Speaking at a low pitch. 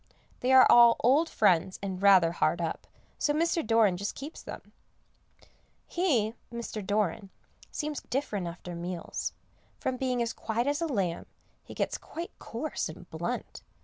No: high, 225 Hz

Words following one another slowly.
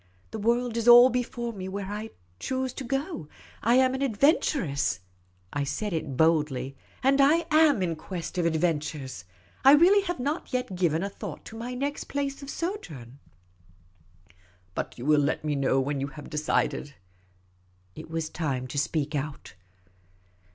No: average, 170 wpm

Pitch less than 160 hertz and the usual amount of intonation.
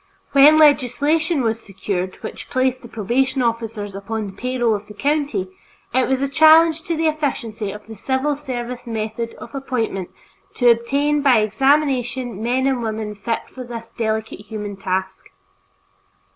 No: high, 240 Hz; average, 4.0 semitones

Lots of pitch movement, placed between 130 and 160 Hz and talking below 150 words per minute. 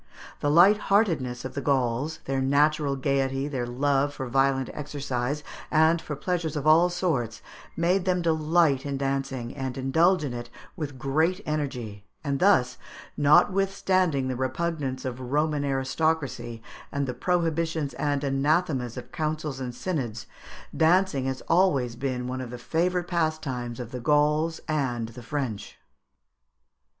No: average, 3.7 semitones; medium, 140 Hz; average, 140 wpm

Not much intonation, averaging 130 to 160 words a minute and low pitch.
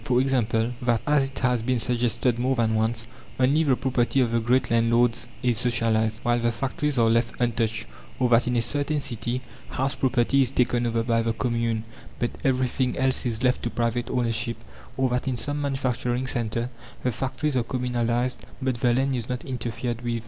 No: narrow, 1.8 semitones; average, 190 wpm; low, 120 Hz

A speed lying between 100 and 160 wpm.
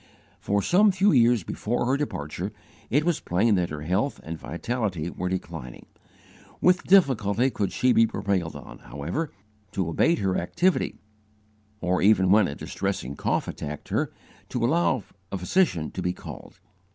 Yes: average, 155 wpm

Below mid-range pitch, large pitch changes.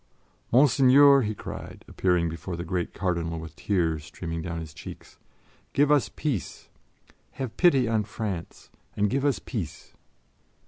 Yes: low, 100 Hz; wide, 7.6 semitones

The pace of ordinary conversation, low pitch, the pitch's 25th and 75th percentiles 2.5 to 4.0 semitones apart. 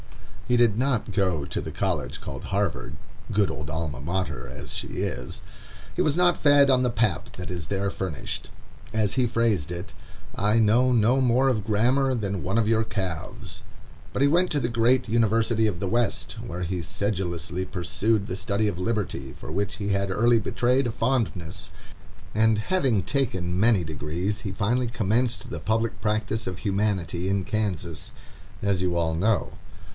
No: average, 175 wpm; low, 105 Hz; average, 4.4 semitones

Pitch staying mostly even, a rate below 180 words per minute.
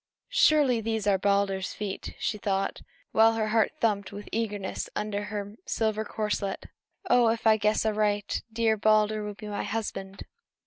Yes: narrow, 1.5 semitones; average, 155 wpm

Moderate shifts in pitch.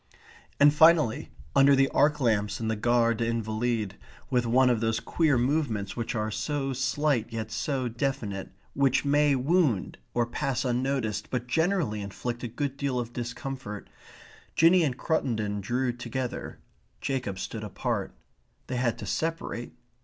Yes: average, 3.6 semitones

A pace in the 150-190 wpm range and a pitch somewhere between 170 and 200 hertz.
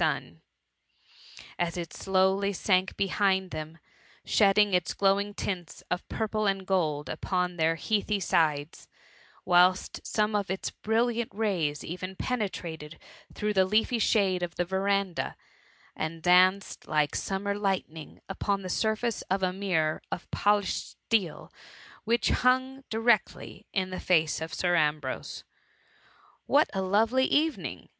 No: slow, 135 wpm; high, 190 Hz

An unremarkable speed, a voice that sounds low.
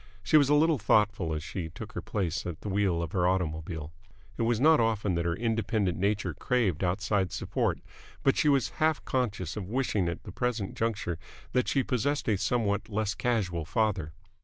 Yes: average, 190 wpm; low, 105 Hz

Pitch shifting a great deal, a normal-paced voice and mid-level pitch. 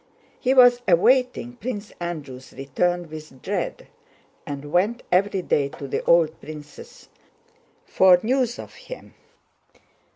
No: wide, 7.9 semitones; slow, 120 wpm; medium, 175 Hz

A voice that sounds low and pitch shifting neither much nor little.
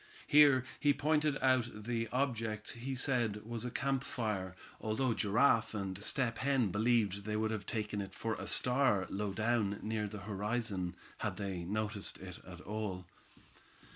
Yes: low, 110 Hz; average, 3.4 semitones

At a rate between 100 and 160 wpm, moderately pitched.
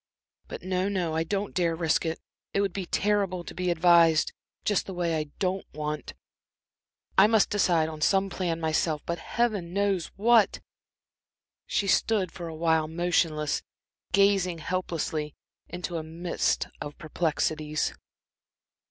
Yes: average, 145 wpm; medium, 175 Hz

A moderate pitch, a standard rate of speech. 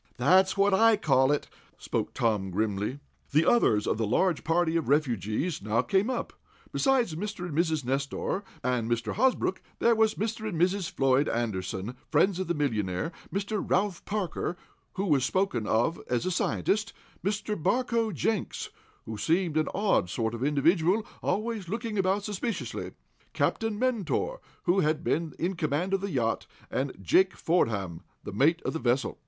Yes: medium, 170 Hz; average, 165 wpm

